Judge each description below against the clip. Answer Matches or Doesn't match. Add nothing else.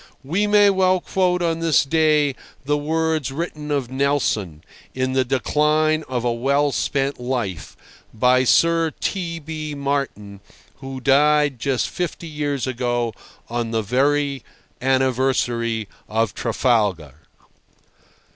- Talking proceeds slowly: Matches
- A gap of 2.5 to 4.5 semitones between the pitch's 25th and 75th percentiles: Matches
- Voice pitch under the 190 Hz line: Matches